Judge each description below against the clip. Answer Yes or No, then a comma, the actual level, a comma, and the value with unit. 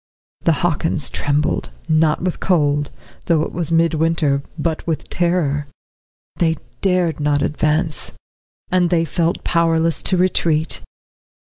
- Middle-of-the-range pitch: Yes, medium, 165 Hz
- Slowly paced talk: Yes, slow, 125 wpm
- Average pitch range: No, narrow, 2.1 semitones